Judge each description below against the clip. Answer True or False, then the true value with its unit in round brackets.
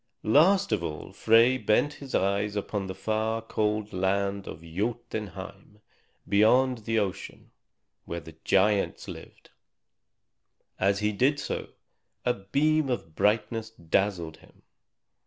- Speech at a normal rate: False (125 wpm)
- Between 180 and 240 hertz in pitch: False (105 Hz)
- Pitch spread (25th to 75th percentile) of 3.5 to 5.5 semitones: False (3.0 semitones)